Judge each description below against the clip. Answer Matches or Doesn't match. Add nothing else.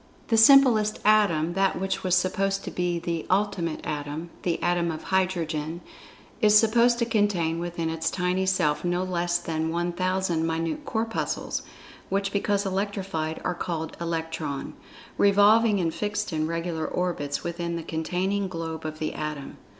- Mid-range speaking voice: Matches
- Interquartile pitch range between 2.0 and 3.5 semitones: Matches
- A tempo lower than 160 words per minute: Matches